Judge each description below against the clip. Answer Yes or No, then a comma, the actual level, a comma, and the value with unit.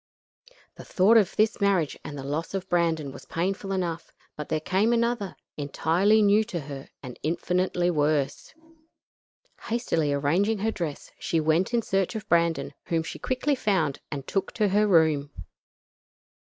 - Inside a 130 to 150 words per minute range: No, average, 160 wpm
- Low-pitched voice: No, medium, 175 Hz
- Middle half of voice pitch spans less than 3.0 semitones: No, average, 4.8 semitones